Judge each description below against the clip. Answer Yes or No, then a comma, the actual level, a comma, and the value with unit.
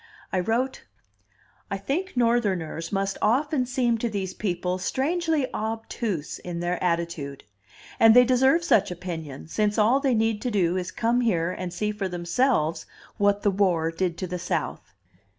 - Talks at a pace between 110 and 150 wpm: No, average, 160 wpm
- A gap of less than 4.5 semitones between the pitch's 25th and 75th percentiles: No, average, 5.3 semitones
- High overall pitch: Yes, high, 205 Hz